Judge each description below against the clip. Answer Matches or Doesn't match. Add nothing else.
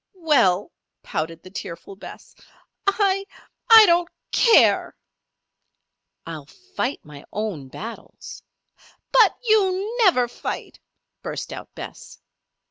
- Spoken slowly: Matches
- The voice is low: Doesn't match